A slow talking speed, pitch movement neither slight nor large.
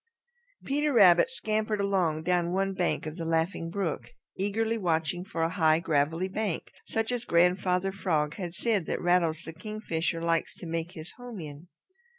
No: average, 165 wpm; average, 3.6 semitones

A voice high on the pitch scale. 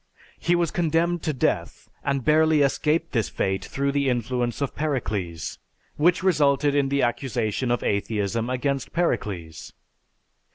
No: low, 135 Hz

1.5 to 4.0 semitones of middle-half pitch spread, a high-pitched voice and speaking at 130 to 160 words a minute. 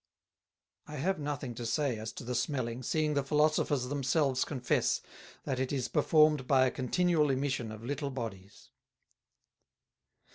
No: average, 3.2 semitones; low, 135 Hz; average, 145 wpm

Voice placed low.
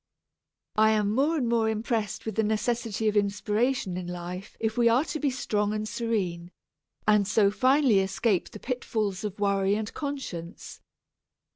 No: high, 215 Hz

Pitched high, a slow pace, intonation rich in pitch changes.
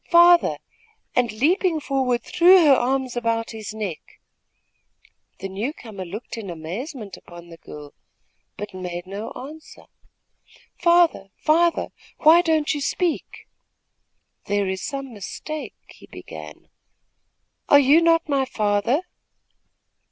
Yes: very high, 250 Hz; slow, 120 wpm; wide, 7.5 semitones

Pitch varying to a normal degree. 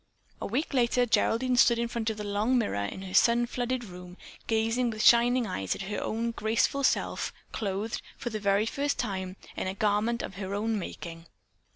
Yes: average, 3.2 semitones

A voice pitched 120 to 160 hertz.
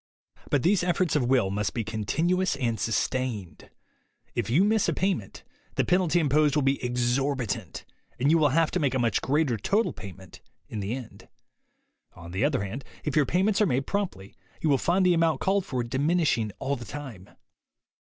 Yes: low, 135 Hz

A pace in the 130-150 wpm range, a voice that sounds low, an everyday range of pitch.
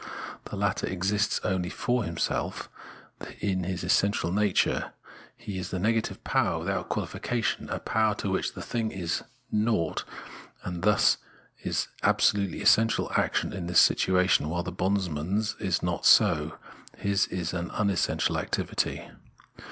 Yes: average, 145 wpm; very low, 95 Hz; average, 3.0 semitones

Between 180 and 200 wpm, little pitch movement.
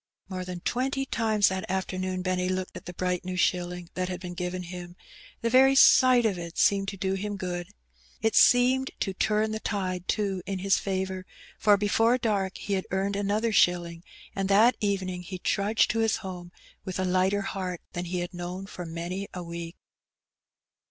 Yes: average, 190 wpm; narrow, 2.3 semitones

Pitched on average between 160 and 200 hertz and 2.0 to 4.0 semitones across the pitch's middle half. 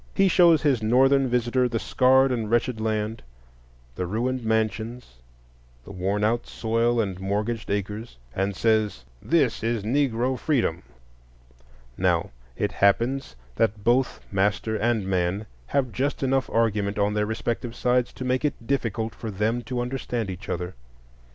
No: low, 115 Hz; average, 3.3 semitones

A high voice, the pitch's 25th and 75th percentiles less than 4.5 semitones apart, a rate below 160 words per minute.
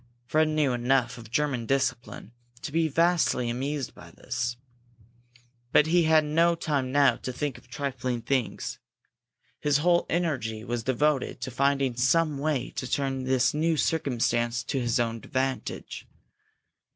No: low, 135 Hz; average, 3.8 semitones; average, 145 wpm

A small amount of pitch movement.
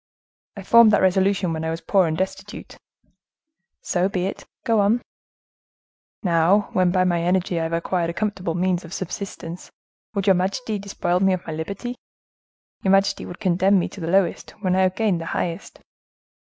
Yes: narrow, 2.3 semitones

